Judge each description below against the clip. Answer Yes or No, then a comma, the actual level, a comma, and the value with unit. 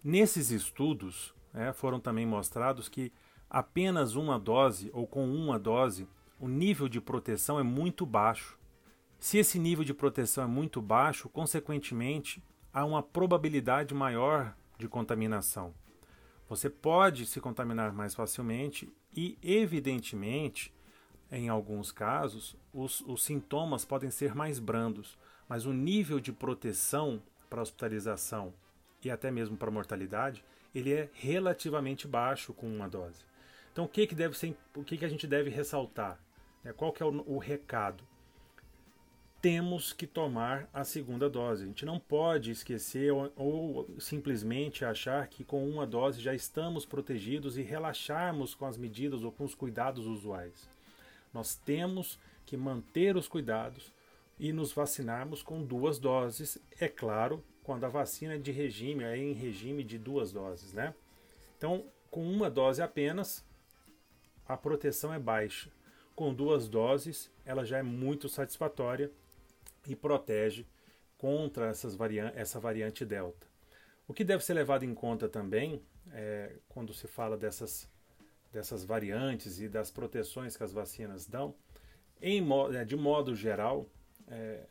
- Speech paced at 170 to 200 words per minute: No, average, 145 wpm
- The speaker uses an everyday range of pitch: Yes, average, 4.7 semitones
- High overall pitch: No, low, 130 Hz